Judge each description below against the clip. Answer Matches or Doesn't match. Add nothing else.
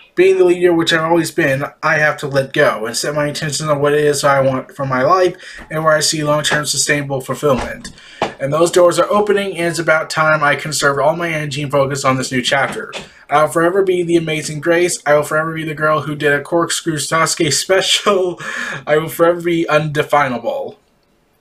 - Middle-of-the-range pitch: Matches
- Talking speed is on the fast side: Matches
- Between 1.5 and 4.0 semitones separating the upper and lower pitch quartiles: Matches